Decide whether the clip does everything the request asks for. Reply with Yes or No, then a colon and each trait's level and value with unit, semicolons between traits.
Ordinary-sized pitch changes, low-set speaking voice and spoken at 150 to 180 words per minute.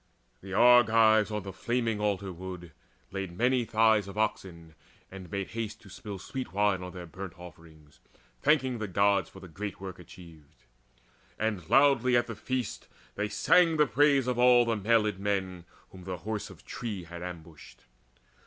Yes: average, 4.1 semitones; low, 100 Hz; average, 170 wpm